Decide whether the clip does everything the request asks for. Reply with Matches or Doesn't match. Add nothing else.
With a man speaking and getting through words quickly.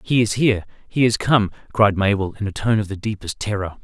Matches